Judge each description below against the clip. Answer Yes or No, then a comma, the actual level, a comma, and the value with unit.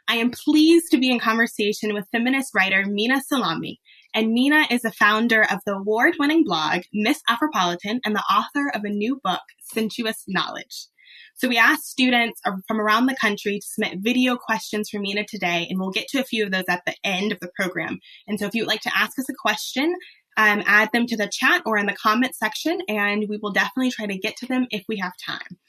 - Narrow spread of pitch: No, average, 3.8 semitones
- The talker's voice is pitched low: No, high, 220 Hz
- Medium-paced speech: No, fast, 225 wpm